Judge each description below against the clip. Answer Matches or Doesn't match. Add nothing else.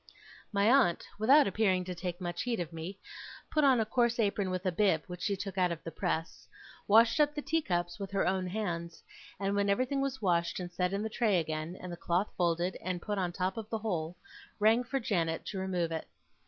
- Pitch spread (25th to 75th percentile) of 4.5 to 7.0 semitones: Doesn't match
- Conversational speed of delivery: Doesn't match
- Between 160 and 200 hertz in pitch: Matches